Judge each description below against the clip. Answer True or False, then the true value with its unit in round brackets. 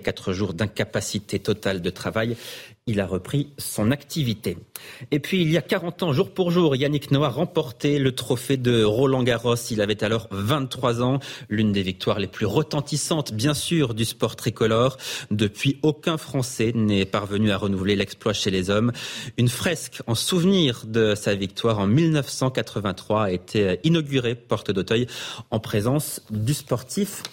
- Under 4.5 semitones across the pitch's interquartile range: False (5.2 semitones)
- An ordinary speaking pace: True (160 wpm)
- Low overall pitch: True (120 Hz)